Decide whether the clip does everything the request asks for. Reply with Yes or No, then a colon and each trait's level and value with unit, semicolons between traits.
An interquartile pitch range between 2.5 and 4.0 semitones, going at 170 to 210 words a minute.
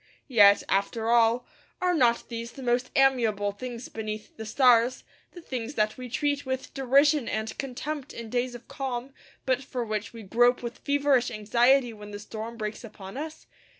Yes: average, 3.1 semitones; average, 175 wpm